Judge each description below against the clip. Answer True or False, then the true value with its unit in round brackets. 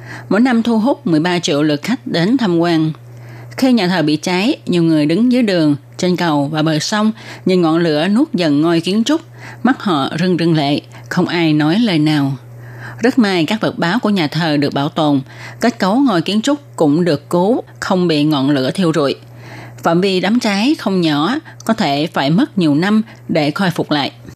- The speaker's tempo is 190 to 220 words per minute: True (210 wpm)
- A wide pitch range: True (6.3 semitones)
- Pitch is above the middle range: False (170 Hz)